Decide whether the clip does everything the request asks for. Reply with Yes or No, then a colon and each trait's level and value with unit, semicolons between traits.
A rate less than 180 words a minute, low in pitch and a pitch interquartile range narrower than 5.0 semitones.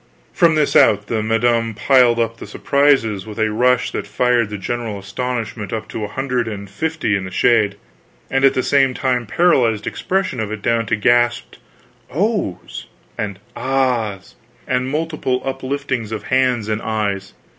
Yes: average, 165 wpm; low, 120 Hz; average, 3.6 semitones